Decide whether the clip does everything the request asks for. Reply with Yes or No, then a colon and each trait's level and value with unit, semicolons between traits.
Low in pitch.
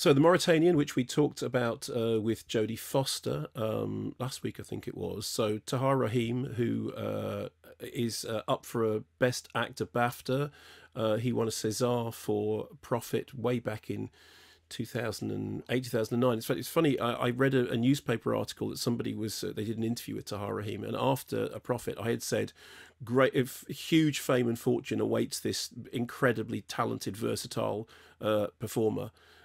Yes: low, 120 Hz